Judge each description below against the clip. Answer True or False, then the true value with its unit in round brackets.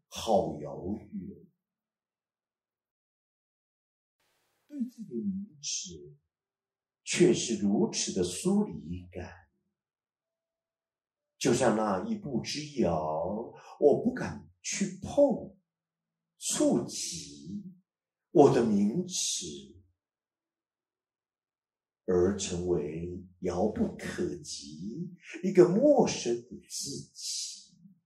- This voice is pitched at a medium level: True (180 Hz)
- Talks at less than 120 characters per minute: True (105 characters per minute)